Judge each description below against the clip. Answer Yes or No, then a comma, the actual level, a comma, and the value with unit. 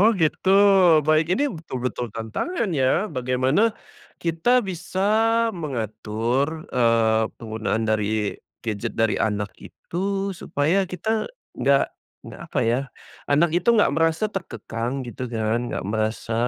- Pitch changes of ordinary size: No, wide, 7.7 semitones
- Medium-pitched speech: No, low, 130 Hz